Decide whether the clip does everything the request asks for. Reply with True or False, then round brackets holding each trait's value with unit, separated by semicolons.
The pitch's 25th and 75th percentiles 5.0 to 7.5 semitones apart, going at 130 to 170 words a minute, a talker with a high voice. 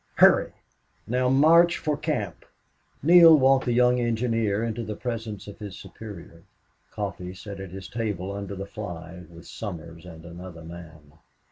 False (5.5 semitones; 145 wpm; 105 Hz)